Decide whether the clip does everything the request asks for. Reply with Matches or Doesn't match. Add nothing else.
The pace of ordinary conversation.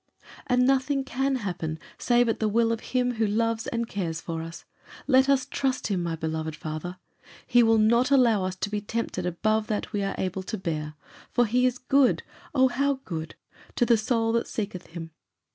Matches